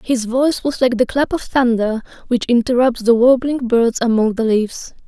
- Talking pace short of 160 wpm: No, average, 190 wpm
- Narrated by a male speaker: No, female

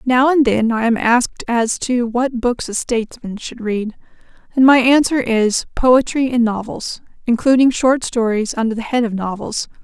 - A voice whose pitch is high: Yes, high, 240 Hz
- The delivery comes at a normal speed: Yes, average, 170 wpm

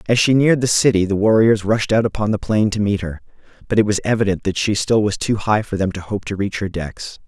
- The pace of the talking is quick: Yes, fast, 270 wpm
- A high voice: No, low, 105 Hz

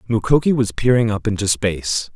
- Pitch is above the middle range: No, low, 115 Hz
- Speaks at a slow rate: No, average, 165 wpm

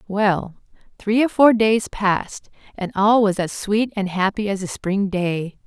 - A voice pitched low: No, high, 200 Hz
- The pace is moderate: Yes, average, 180 wpm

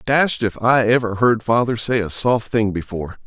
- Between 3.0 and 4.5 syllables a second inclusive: No, 4.9 syllables/s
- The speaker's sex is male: Yes, male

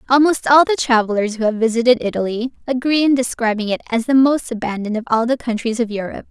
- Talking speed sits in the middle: No, fast, 210 wpm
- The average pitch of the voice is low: No, high, 240 Hz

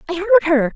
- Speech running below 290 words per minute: Yes, fast, 240 wpm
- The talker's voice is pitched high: Yes, very high, 340 Hz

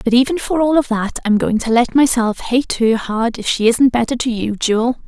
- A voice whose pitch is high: Yes, high, 240 Hz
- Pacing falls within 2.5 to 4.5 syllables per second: No, 5.0 syllables/s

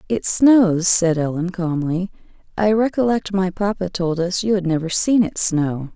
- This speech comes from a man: No, female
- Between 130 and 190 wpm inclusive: Yes, average, 170 wpm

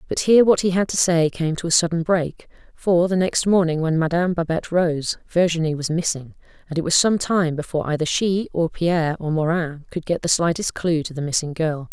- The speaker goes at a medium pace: No, fast, 220 wpm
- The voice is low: No, medium, 165 Hz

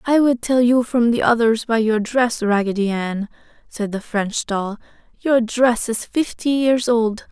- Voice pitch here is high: Yes, high, 230 Hz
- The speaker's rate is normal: Yes, average, 180 wpm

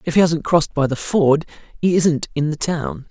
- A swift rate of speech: Yes, fast, 230 wpm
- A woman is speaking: No, male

